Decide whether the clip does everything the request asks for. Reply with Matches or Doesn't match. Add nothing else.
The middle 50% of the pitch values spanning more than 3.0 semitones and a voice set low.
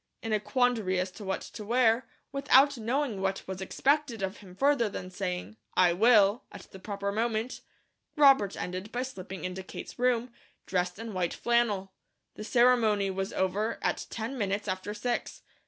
Doesn't match